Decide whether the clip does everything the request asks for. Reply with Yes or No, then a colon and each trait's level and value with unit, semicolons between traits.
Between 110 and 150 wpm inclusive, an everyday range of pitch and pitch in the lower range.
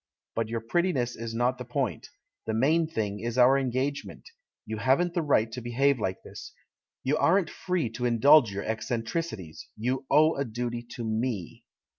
No: average, 175 wpm; average, 3.8 semitones; low, 125 Hz